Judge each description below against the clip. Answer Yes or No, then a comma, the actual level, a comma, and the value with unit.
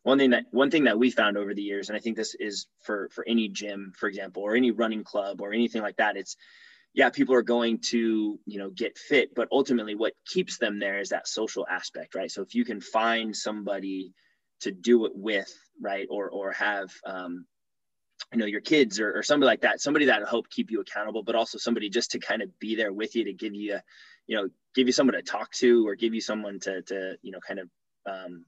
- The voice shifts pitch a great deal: No, average, 2.7 semitones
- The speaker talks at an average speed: No, fast, 240 wpm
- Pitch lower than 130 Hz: Yes, low, 110 Hz